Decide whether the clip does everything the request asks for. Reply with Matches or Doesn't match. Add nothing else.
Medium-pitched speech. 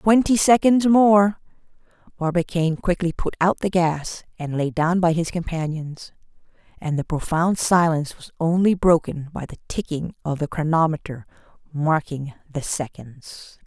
Matches